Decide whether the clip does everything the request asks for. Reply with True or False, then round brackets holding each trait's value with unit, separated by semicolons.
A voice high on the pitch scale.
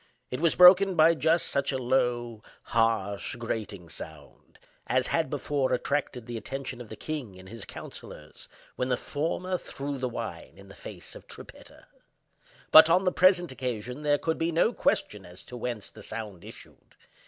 False (125 Hz)